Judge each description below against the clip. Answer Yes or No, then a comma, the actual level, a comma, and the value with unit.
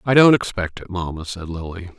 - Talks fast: Yes, fast, 210 wpm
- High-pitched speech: No, very low, 95 Hz